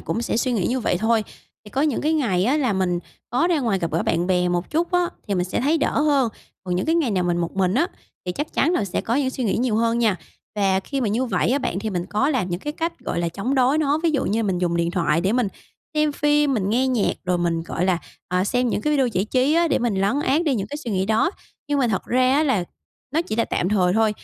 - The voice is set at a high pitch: Yes, high, 230 Hz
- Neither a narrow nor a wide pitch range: No, wide, 6.8 semitones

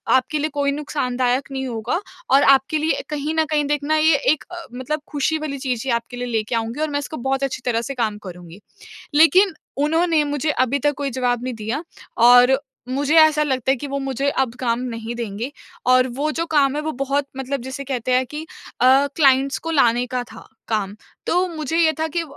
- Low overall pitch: No, very high, 270 Hz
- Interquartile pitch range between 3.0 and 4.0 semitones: Yes, average, 3.4 semitones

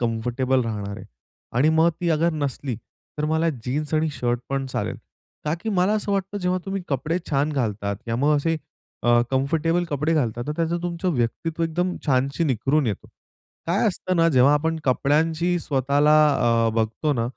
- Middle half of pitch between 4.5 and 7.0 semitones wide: Yes, average, 4.8 semitones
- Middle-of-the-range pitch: Yes, medium, 150 Hz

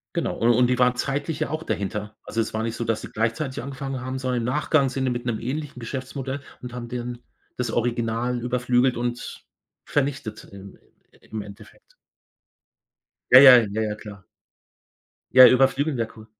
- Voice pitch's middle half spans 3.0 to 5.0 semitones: No, narrow, 2.6 semitones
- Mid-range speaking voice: No, low, 125 Hz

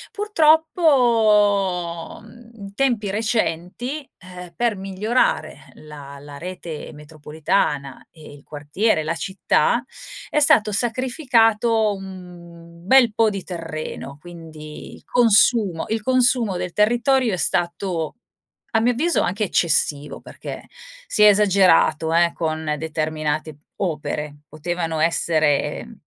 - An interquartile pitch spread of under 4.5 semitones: No, wide, 6.0 semitones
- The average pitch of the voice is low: No, medium, 185 Hz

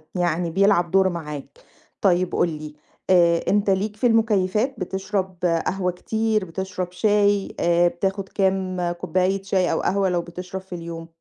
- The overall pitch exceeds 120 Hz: Yes, medium, 185 Hz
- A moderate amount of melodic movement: No, narrow, 2.2 semitones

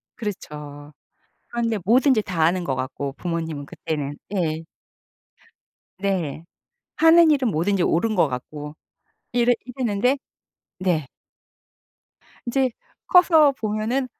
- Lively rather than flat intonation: Yes, wide, 8.0 semitones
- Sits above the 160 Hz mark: Yes, high, 190 Hz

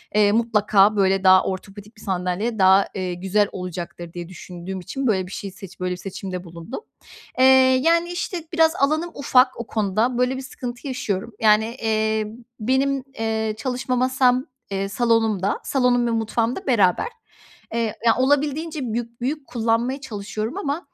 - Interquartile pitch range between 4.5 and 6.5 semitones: Yes, average, 4.8 semitones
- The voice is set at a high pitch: Yes, high, 225 Hz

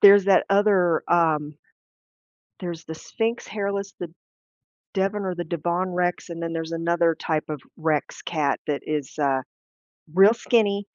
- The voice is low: No, medium, 175 Hz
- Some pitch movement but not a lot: Yes, average, 3.7 semitones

